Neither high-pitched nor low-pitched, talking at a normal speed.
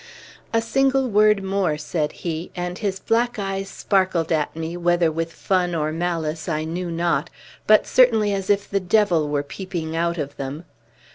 Yes: medium, 175 Hz; average, 170 wpm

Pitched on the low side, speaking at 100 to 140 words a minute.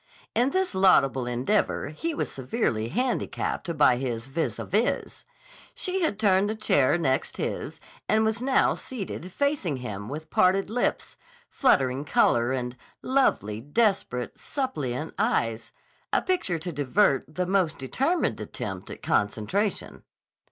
No: medium, 170 Hz; slow, 135 wpm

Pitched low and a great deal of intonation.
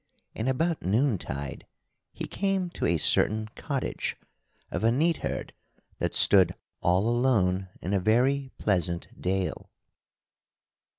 Yes: low, 110 Hz; wide, 6.6 semitones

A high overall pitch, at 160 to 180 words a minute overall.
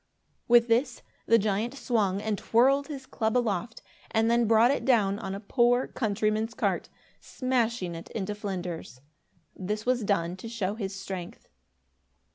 No: high, 220 Hz; average, 150 wpm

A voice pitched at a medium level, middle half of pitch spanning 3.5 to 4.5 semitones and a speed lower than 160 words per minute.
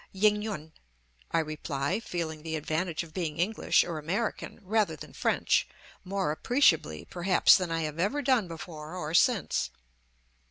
Yes: medium, 170 Hz; average, 4.1 semitones; average, 150 wpm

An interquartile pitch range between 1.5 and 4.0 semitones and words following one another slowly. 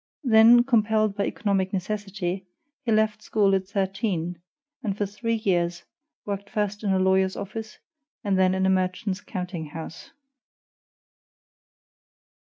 Yes: narrow, 2.4 semitones; slow, 130 wpm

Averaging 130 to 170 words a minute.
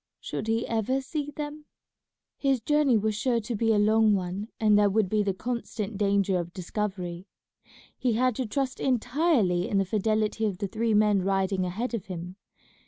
No: average, 180 wpm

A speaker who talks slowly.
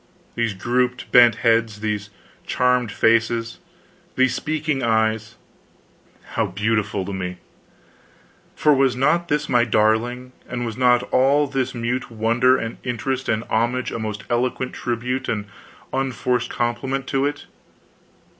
Yes: slow, 130 wpm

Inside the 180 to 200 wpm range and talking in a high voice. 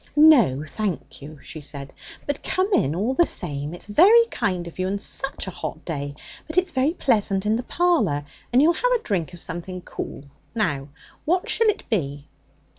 Yes: average, 190 wpm; high, 200 Hz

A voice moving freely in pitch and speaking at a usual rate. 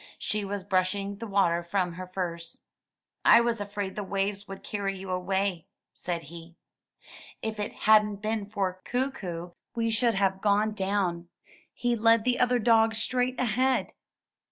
No: average, 3.2 semitones; average, 155 wpm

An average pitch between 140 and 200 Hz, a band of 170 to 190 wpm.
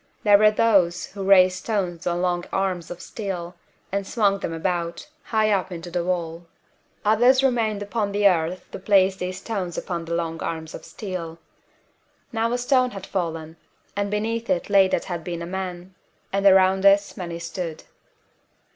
Yes: high, 190 Hz; average, 175 wpm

